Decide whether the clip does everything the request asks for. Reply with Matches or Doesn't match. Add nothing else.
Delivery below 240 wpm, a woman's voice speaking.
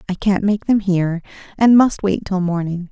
Matches